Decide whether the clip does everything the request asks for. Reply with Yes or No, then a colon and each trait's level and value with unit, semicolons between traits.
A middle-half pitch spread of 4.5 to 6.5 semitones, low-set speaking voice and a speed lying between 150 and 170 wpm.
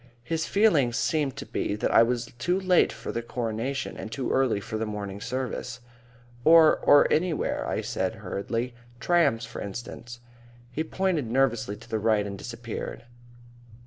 Yes: average, 5.1 semitones; low, 120 Hz; average, 160 wpm